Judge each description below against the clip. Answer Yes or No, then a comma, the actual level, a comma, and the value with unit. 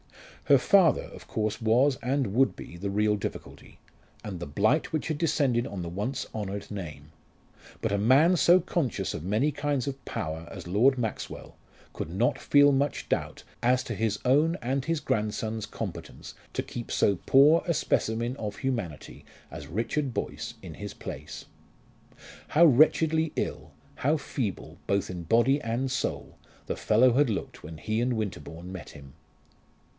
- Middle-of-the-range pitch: No, low, 120 Hz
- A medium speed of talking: Yes, average, 165 wpm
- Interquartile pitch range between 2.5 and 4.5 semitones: No, wide, 5.6 semitones